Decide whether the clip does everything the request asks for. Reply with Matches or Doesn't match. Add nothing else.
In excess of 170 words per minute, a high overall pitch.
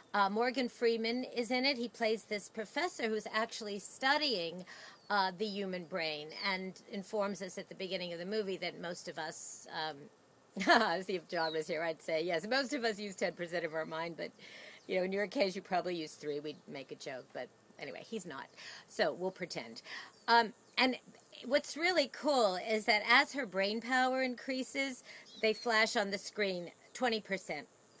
Matches